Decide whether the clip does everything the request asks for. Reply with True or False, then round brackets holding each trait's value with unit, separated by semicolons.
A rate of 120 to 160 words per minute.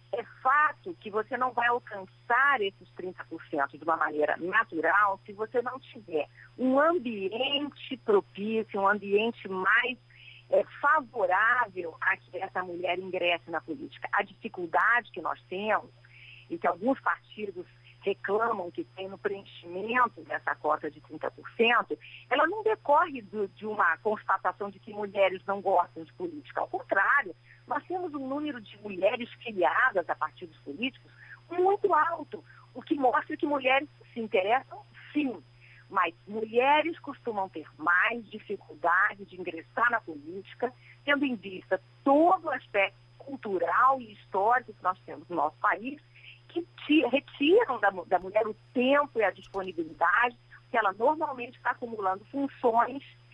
True (140 wpm)